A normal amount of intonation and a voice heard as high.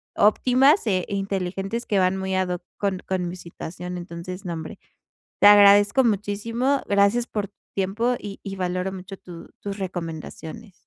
No: narrow, 2.2 semitones; high, 195 Hz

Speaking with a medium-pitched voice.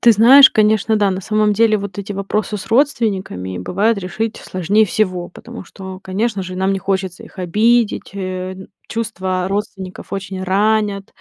No: high, 200 Hz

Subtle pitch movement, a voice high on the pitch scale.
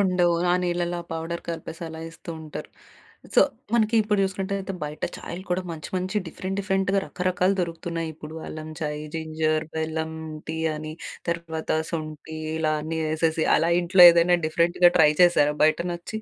No: narrow, 2.2 semitones; medium, 170 Hz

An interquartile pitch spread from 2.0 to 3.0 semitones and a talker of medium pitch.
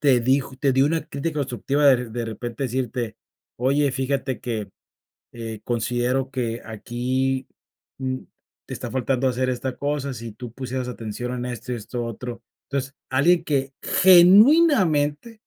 No: narrow, 2.5 semitones; low, 130 Hz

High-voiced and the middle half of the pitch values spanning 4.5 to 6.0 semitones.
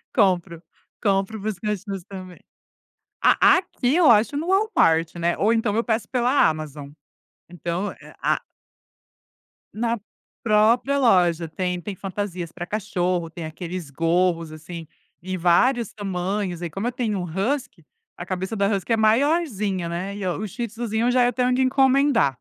Yes: high, 195 Hz; average, 5.1 semitones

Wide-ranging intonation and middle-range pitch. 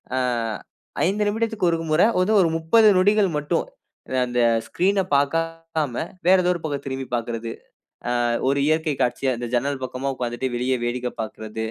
Yes: wide, 6.4 semitones; medium, 145 Hz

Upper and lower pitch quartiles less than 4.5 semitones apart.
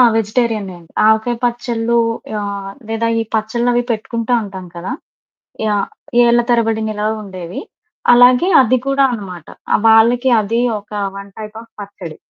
Yes: average, 2.8 semitones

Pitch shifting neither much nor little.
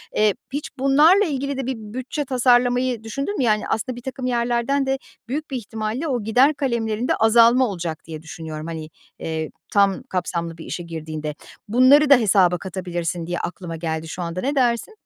No: wide, 7.0 semitones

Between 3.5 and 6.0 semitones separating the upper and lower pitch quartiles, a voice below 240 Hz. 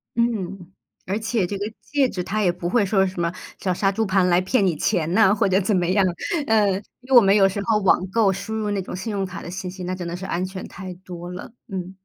No: narrow, 2.6 semitones; high, 190 Hz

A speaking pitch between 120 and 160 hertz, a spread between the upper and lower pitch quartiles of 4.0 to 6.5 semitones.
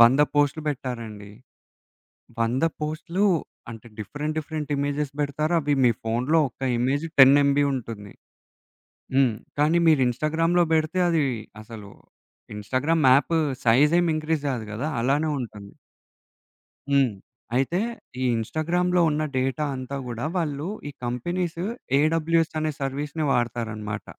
Yes: medium, 140 Hz; average, 4.5 semitones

